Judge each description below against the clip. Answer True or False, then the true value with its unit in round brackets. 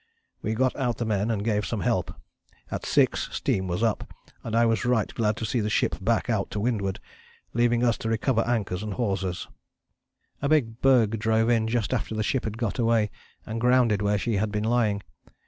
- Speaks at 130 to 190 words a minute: False (205 wpm)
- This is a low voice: True (110 Hz)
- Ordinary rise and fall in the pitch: False (2.1 semitones)